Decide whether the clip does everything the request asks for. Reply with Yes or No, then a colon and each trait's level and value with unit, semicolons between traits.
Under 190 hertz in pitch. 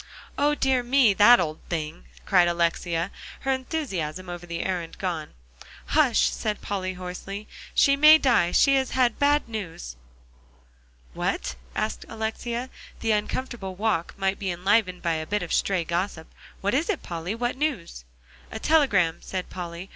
No: high, 195 Hz